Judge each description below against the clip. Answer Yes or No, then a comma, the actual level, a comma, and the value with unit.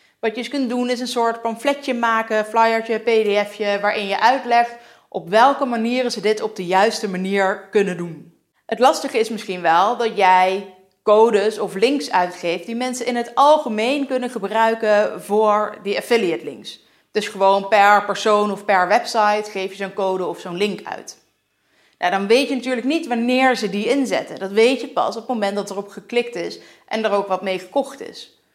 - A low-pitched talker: No, high, 215 Hz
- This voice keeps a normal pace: Yes, average, 190 wpm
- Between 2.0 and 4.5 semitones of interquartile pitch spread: Yes, average, 3.2 semitones